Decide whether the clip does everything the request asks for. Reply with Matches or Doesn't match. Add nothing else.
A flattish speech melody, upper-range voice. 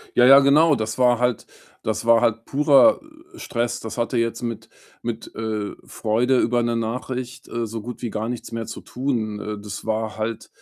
Doesn't match